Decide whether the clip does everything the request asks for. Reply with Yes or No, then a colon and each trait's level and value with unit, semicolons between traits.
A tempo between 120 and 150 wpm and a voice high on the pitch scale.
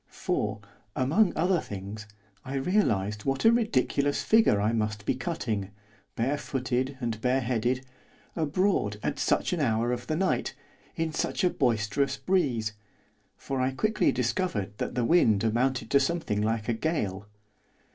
No: average, 145 wpm; low, 130 Hz